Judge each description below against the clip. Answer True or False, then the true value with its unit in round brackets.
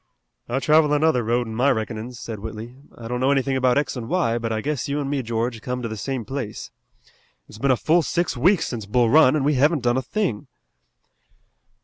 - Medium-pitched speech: False (125 Hz)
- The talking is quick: True (225 wpm)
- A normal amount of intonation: True (3.8 semitones)